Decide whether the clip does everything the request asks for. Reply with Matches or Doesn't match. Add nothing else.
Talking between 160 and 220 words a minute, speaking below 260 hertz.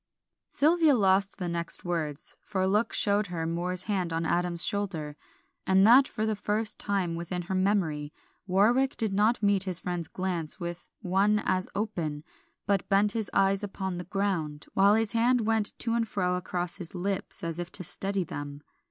Matches